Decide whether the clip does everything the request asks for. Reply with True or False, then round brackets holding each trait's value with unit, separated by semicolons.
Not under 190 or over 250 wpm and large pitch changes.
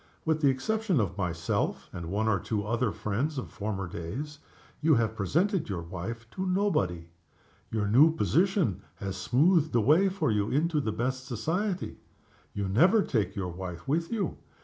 False (170 wpm; 8.4 semitones)